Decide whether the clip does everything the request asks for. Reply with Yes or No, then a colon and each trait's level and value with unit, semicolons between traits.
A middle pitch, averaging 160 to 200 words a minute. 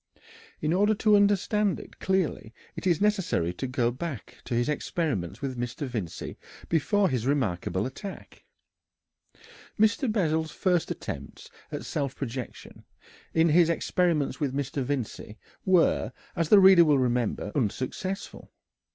No: medium, 150 Hz; slow, 135 wpm